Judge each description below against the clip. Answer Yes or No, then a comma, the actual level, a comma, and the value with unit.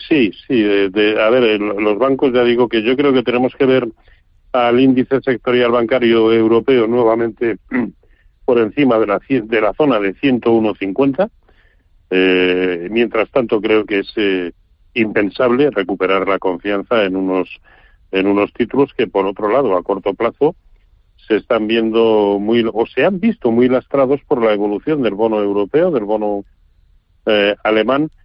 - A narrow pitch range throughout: No, average, 4.0 semitones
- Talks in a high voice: No, low, 110 Hz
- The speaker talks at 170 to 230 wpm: No, average, 160 wpm